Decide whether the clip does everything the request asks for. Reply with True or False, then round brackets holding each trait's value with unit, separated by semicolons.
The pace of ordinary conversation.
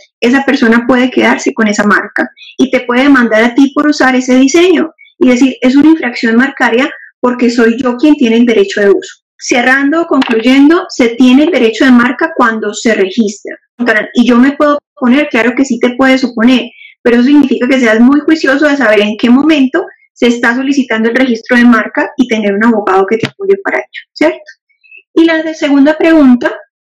False (195 wpm)